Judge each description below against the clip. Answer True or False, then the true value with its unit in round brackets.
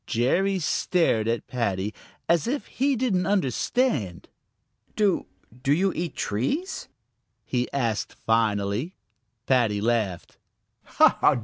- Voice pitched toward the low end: True (130 Hz)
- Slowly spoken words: True (100 wpm)